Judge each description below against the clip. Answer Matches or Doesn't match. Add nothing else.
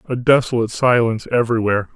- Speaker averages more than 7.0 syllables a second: Matches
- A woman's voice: Doesn't match